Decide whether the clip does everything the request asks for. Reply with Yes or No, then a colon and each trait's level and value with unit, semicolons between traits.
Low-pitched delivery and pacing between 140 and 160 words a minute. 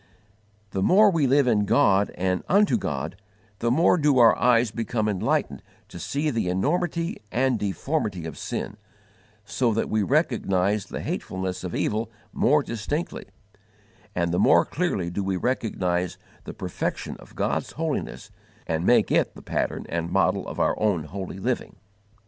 Yes: low, 110 Hz; average, 155 wpm